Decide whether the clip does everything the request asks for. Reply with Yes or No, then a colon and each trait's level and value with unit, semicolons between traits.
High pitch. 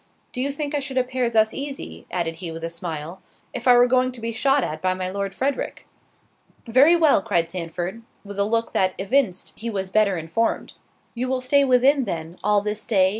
Yes: high, 220 Hz